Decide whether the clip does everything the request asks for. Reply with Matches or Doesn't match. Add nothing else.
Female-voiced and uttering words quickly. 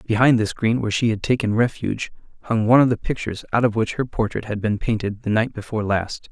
Doesn't match